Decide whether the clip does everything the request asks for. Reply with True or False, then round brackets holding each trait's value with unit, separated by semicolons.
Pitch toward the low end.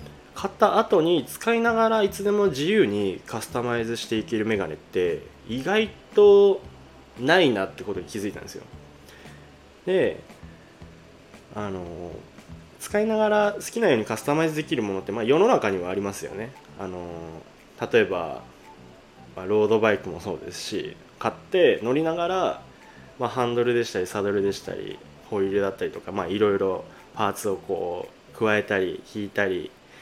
True (105 Hz)